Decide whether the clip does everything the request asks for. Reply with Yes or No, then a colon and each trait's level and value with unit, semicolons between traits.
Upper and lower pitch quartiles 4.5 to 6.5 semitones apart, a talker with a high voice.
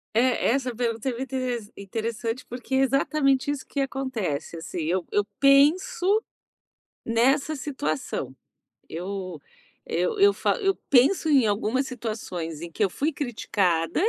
Yes: wide, 5.4 semitones; high, 245 Hz